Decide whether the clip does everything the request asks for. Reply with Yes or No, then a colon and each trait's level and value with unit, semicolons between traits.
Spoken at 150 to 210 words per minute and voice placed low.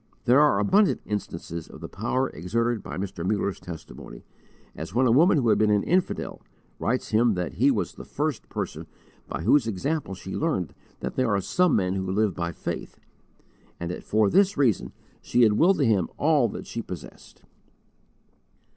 Yes: average, 180 wpm; low, 110 Hz